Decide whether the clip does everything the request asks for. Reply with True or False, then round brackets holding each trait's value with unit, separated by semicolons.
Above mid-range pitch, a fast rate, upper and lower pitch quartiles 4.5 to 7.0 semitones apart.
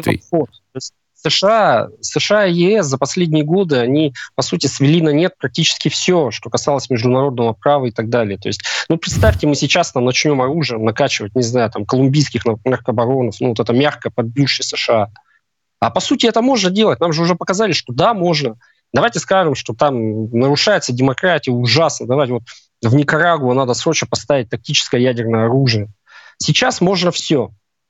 False (140 Hz; 165 wpm; 5.2 semitones)